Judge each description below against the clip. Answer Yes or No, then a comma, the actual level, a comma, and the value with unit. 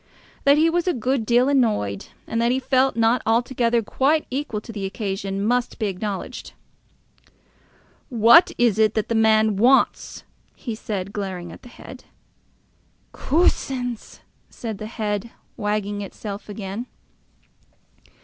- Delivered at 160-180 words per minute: No, slow, 135 wpm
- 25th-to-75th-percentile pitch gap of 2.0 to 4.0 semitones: Yes, average, 3.3 semitones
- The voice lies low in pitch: No, high, 225 Hz